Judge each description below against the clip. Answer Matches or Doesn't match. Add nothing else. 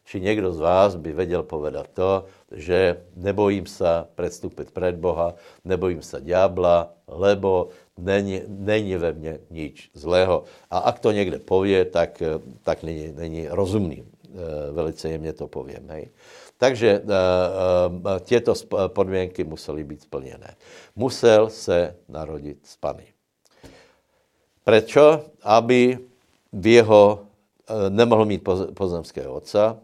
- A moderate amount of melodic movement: Matches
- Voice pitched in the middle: Doesn't match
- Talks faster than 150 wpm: Doesn't match